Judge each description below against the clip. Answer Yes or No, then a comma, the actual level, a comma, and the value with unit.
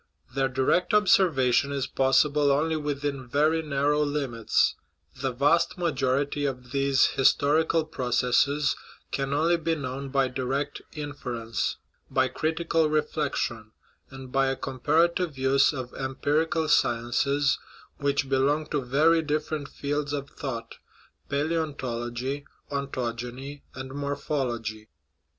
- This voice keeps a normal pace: No, slow, 115 wpm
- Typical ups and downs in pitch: No, narrow, 2.3 semitones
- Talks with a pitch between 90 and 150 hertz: Yes, medium, 140 Hz